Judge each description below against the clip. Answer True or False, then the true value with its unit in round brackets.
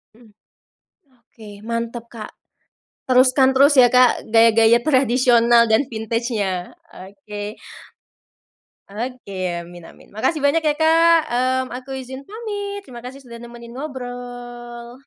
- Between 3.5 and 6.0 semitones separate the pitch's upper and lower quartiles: False (2.5 semitones)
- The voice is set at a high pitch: True (245 Hz)